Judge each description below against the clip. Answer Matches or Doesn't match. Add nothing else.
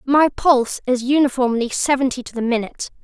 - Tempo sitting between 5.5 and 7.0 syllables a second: Matches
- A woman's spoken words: Matches